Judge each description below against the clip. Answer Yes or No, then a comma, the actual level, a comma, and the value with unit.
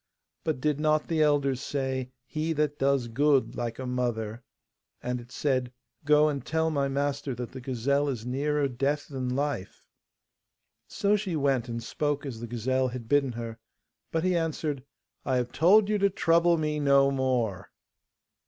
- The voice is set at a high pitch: No, medium, 140 Hz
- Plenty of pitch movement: No, average, 3.2 semitones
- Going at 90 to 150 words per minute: No, average, 170 wpm